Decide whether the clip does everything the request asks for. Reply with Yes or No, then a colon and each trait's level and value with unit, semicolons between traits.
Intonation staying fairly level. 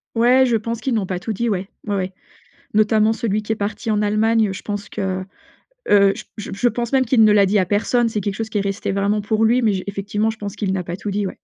Yes: narrow, 2.1 semitones